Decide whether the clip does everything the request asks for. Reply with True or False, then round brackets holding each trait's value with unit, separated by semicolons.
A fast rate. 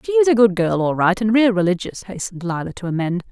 True (255 wpm)